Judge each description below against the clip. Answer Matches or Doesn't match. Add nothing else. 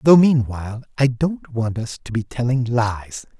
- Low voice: Matches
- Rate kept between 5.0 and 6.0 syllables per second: Doesn't match